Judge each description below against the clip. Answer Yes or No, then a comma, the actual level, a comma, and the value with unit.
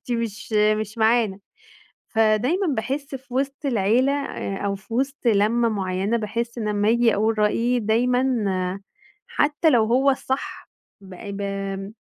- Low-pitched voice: No, high, 225 Hz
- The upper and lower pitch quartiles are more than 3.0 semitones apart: Yes, average, 3.5 semitones